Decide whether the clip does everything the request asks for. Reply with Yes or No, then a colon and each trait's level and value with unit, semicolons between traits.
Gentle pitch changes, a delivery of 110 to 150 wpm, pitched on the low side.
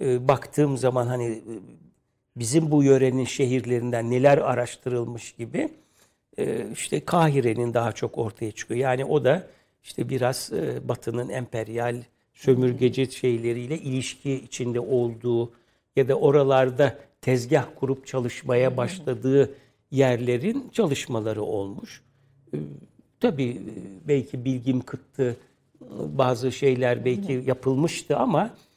No: narrow, 2.1 semitones; average, 100 wpm; low, 130 Hz